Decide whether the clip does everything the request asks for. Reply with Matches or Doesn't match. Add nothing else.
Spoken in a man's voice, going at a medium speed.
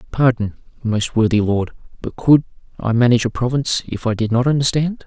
Matches